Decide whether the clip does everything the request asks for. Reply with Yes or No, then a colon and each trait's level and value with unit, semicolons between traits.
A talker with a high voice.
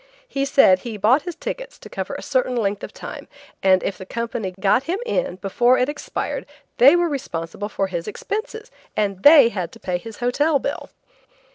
Yes: high, 240 Hz